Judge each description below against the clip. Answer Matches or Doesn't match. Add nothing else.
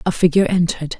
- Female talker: Matches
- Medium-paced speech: Matches